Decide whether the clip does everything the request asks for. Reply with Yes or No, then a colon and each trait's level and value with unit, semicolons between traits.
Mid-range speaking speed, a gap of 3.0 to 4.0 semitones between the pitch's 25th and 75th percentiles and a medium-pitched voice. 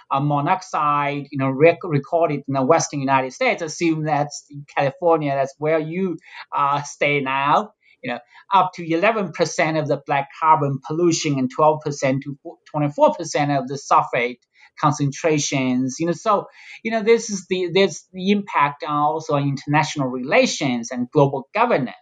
Yes: average, 160 wpm; average, 3.3 semitones; medium, 150 Hz